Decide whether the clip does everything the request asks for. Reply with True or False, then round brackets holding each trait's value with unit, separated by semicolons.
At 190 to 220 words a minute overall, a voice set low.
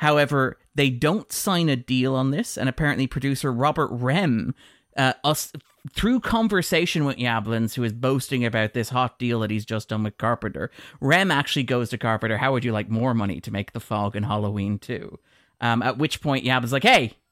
True (200 wpm; 130 Hz)